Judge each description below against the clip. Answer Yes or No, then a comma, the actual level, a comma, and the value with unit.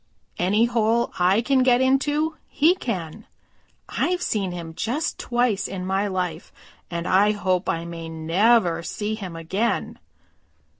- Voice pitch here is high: Yes, high, 205 Hz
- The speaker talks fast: No, average, 140 wpm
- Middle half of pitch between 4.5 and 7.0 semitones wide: Yes, average, 5.2 semitones